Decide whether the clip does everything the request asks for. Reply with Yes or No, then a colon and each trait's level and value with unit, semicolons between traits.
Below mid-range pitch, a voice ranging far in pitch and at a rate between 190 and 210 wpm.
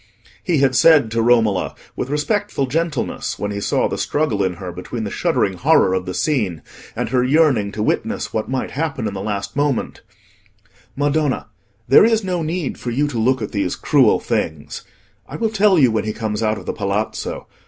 Yes: low, 125 Hz; wide, 6.2 semitones; average, 195 wpm